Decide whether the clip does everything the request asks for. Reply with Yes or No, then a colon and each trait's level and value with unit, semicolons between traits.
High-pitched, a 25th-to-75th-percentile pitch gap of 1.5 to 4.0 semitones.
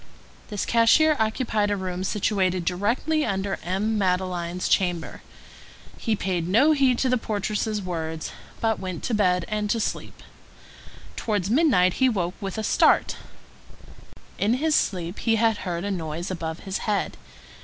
Yes: high, 200 Hz; average, 3.7 semitones